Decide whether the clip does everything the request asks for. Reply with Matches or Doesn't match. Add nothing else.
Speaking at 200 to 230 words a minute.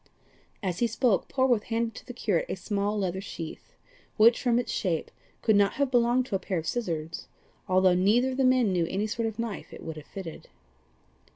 Matches